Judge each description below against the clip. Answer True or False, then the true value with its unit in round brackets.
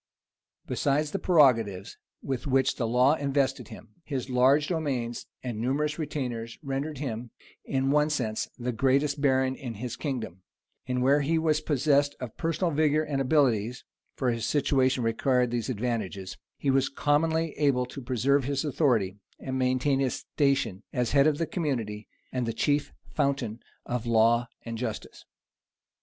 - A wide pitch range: False (3.3 semitones)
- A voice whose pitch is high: False (130 Hz)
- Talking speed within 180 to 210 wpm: False (155 wpm)